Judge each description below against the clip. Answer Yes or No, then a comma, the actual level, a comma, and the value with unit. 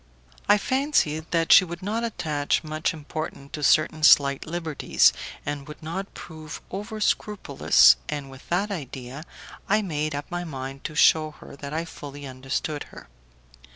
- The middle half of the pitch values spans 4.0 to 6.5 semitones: No, average, 3.6 semitones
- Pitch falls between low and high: Yes, medium, 155 Hz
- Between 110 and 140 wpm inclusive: No, average, 155 wpm